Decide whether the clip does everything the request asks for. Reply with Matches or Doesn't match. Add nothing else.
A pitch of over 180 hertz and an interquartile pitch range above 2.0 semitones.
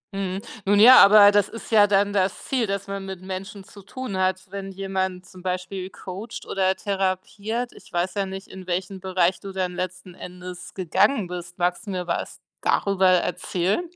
Doesn't match